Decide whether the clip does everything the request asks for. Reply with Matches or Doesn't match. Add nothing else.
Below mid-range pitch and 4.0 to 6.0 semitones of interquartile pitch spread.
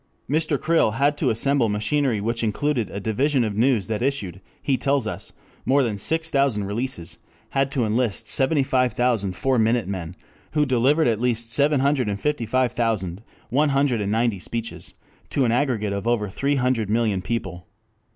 Matches